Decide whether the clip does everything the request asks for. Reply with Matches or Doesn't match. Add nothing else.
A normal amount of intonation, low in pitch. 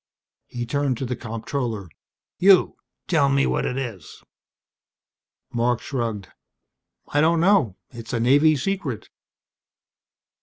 Matches